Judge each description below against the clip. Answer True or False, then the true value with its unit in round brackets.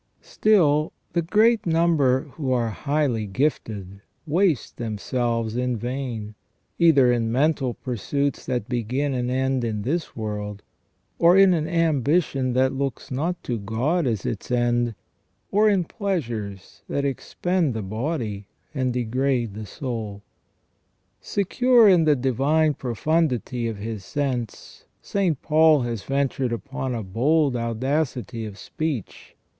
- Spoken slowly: True (130 wpm)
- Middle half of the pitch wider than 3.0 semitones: True (5.1 semitones)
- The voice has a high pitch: False (130 Hz)